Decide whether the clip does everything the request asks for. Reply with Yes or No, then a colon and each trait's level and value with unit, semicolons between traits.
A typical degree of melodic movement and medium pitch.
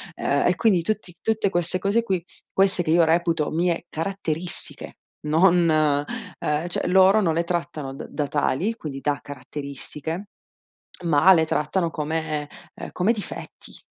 Yes: average, 3.8 semitones; medium, 170 Hz